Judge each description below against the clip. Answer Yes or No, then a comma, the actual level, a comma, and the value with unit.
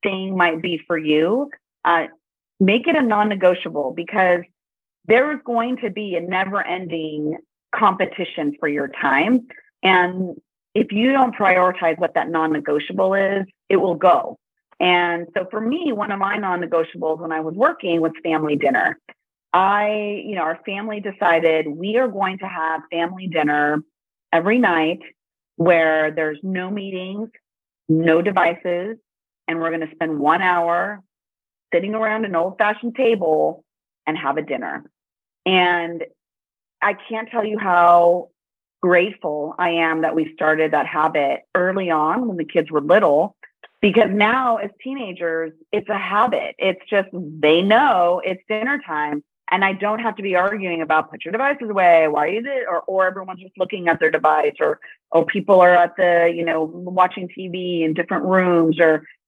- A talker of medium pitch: Yes, medium, 180 Hz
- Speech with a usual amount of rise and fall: Yes, average, 4.0 semitones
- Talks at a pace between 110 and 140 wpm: No, average, 165 wpm